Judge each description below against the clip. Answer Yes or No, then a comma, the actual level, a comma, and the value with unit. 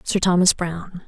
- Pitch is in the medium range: Yes, medium, 180 Hz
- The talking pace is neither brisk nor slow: Yes, average, 170 wpm